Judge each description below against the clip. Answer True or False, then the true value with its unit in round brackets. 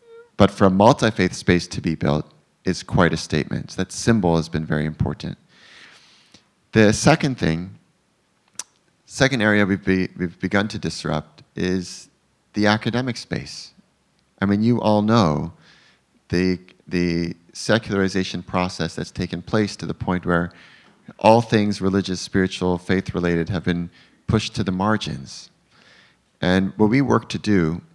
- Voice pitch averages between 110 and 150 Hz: False (95 Hz)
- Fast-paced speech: False (150 wpm)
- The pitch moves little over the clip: False (3.7 semitones)